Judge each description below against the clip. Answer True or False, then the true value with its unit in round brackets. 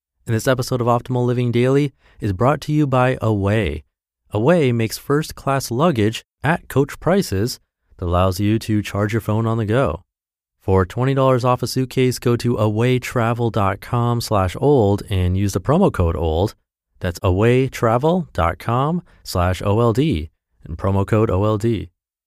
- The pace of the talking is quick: False (140 wpm)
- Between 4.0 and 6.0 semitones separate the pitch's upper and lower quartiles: True (5.1 semitones)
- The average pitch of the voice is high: False (115 Hz)